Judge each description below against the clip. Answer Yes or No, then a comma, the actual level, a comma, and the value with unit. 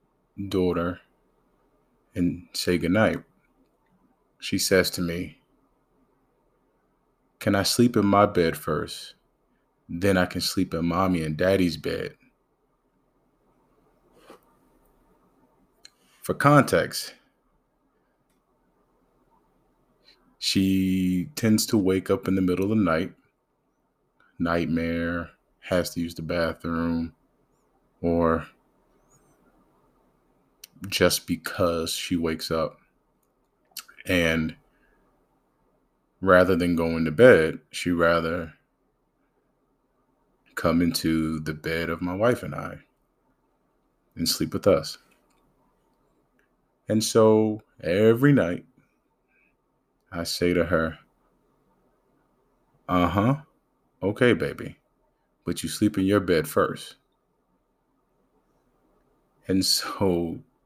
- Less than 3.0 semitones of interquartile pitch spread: Yes, narrow, 2.5 semitones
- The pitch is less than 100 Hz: Yes, very low, 85 Hz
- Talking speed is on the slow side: Yes, slow, 90 wpm